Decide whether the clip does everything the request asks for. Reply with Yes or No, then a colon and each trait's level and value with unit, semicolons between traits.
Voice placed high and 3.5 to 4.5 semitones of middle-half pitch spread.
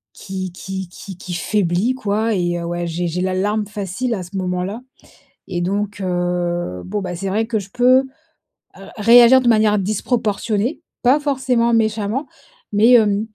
Yes: high, 205 Hz; average, 4.0 semitones